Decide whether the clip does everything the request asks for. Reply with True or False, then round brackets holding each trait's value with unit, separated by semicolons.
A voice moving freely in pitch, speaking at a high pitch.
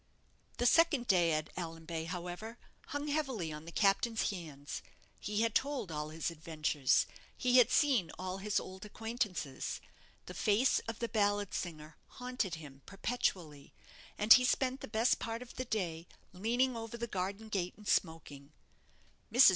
True (6.3 semitones; 200 Hz)